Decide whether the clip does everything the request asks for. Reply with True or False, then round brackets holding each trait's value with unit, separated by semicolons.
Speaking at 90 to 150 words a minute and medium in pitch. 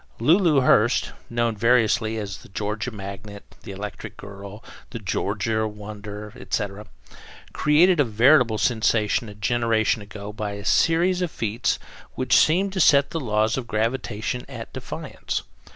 False (140 wpm; 110 Hz)